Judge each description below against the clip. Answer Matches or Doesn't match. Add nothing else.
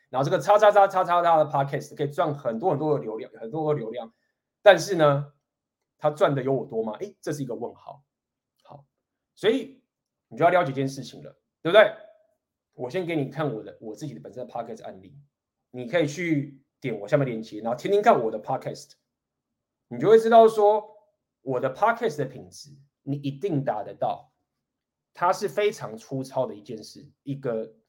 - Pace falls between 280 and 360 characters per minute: Matches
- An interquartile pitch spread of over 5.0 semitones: Matches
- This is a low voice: Doesn't match